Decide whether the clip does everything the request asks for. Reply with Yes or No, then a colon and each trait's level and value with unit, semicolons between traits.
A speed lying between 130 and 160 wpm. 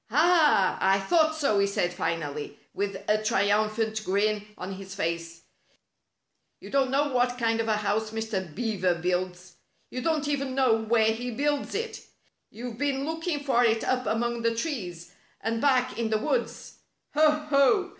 No: average, 170 wpm